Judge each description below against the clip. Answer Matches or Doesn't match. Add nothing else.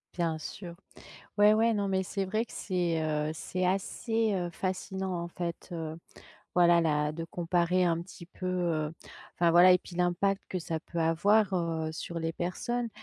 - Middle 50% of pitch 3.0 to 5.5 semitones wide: Doesn't match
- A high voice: Doesn't match